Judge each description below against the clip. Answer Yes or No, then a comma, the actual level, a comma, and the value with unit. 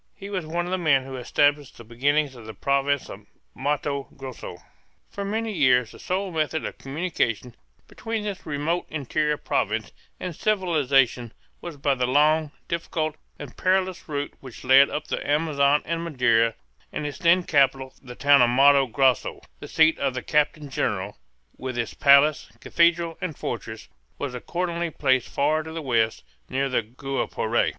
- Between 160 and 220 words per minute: Yes, average, 165 wpm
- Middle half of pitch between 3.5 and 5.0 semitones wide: Yes, average, 4.0 semitones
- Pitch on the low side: No, medium, 145 Hz